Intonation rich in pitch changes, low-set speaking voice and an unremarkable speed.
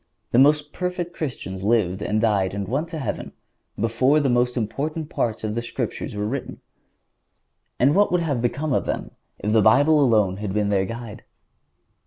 Yes: wide, 5.9 semitones; low, 120 Hz; average, 180 wpm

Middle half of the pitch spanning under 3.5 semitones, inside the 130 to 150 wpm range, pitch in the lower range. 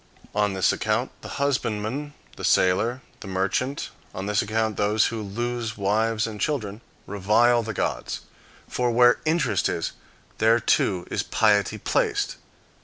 Yes: average, 2.9 semitones; average, 140 wpm; low, 110 Hz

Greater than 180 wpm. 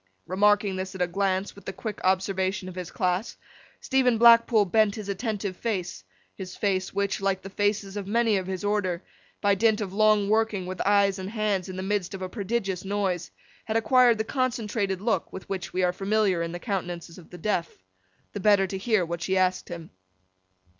Yes: average, 195 wpm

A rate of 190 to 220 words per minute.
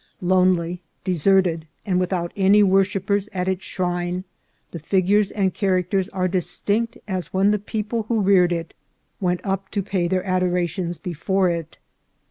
No: average, 155 wpm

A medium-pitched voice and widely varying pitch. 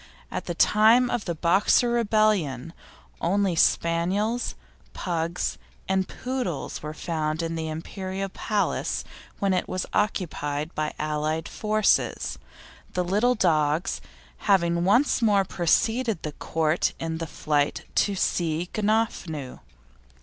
No: medium, 180 Hz; average, 4.6 semitones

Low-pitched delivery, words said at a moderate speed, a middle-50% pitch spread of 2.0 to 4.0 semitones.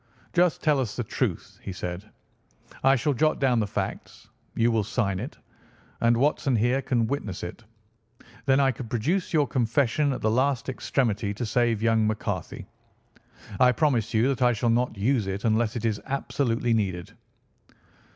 Yes: low, 120 Hz; average, 170 wpm; average, 3.6 semitones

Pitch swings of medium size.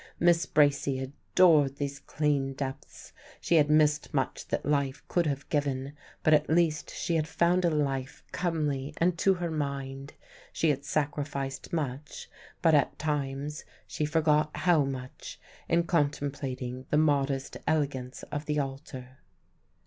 No: narrow, 2.3 semitones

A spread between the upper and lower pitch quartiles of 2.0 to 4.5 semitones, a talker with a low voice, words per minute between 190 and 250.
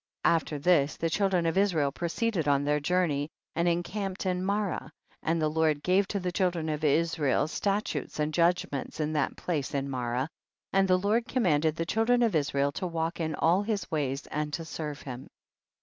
No: average, 3.7 semitones; medium, 165 Hz; average, 195 wpm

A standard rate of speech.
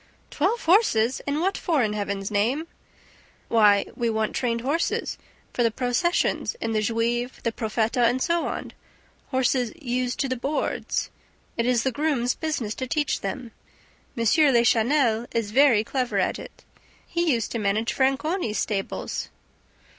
Yes: average, 150 wpm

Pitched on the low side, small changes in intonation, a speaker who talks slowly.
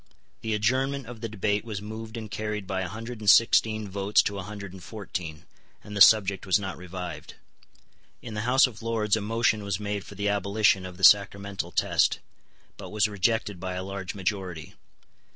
No: low, 105 Hz; narrow, 2.3 semitones; average, 190 wpm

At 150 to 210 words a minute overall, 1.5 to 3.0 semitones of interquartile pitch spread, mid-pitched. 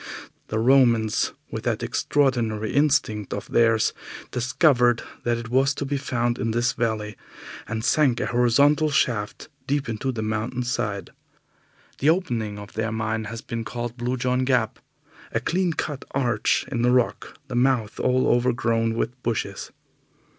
No: average, 155 wpm; average, 2.7 semitones; low, 120 Hz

